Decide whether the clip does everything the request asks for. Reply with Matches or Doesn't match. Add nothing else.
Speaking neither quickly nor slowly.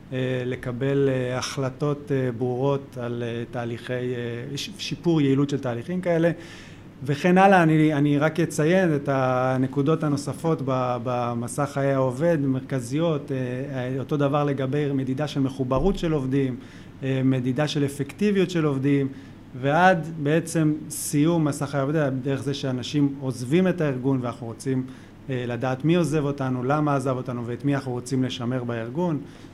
Matches